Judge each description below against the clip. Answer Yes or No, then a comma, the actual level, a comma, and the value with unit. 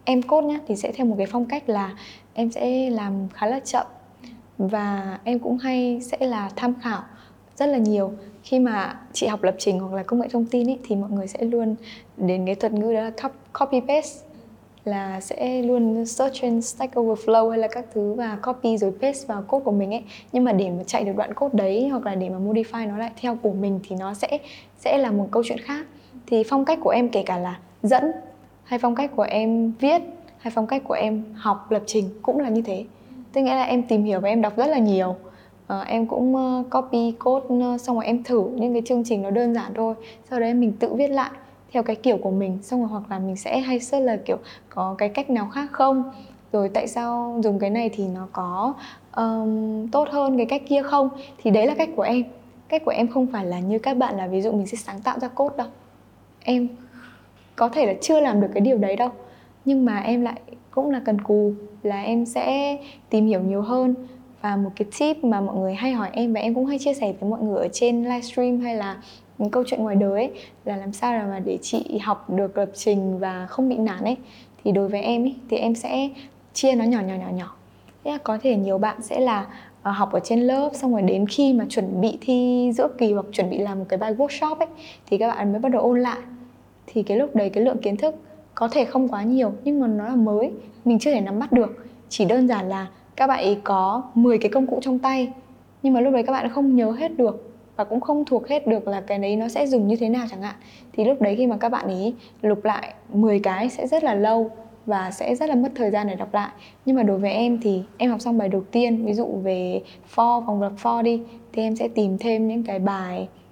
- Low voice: No, high, 230 Hz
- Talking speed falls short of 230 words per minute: No, fast, 250 wpm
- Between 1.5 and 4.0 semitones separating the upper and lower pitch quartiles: Yes, average, 3.6 semitones